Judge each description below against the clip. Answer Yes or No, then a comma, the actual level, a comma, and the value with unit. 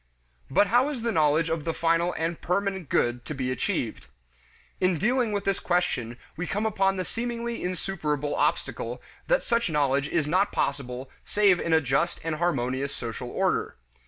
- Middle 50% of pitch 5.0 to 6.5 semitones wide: Yes, wide, 5.5 semitones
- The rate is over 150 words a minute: Yes, average, 170 wpm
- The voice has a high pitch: No, medium, 170 Hz